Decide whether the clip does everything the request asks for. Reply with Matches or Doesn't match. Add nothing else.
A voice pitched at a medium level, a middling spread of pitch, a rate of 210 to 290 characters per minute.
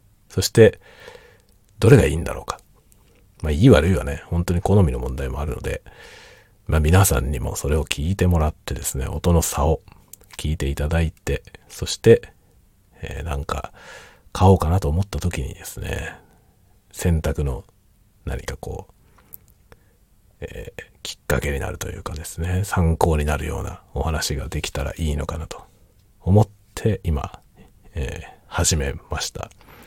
Doesn't match